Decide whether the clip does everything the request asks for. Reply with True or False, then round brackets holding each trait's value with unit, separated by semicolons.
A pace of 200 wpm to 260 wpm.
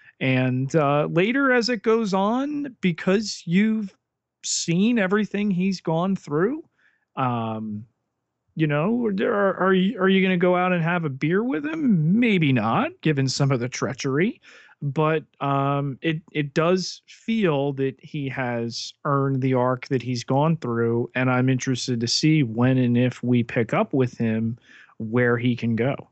False (170 wpm)